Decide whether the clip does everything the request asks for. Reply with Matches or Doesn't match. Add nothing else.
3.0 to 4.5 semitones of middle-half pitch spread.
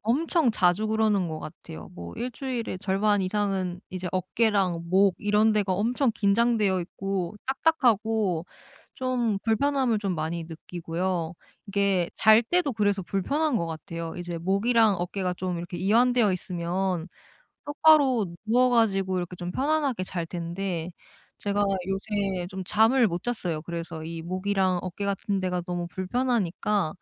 Matches